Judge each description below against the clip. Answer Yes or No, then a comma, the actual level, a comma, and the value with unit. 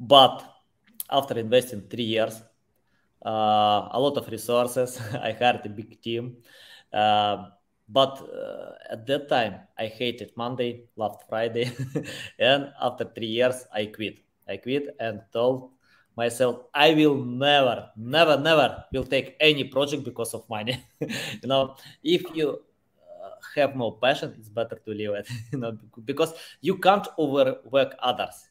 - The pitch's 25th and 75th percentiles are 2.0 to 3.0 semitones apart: No, average, 3.4 semitones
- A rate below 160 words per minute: Yes, average, 145 wpm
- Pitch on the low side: Yes, low, 120 Hz